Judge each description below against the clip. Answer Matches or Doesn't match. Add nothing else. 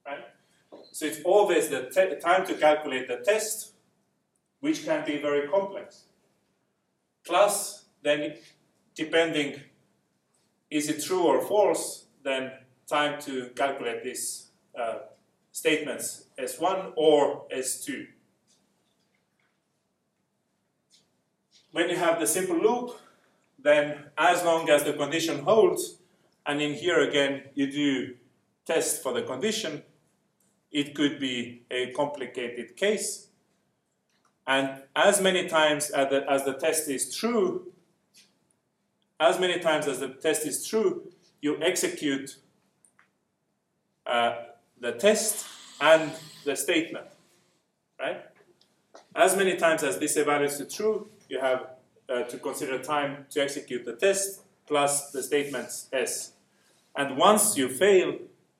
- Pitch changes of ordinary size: Doesn't match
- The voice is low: Doesn't match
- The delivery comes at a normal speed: Doesn't match